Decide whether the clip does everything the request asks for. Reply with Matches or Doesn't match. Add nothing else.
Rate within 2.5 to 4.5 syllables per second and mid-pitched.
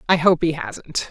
Matches